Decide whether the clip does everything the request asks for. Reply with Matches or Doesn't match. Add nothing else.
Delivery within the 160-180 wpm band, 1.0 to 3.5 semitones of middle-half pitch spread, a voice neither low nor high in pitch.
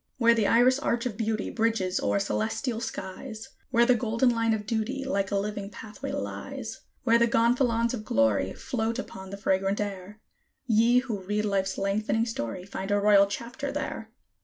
Doesn't match